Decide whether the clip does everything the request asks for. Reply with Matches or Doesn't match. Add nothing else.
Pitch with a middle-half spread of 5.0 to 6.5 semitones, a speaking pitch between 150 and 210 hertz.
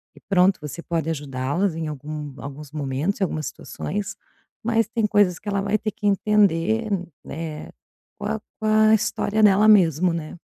Matches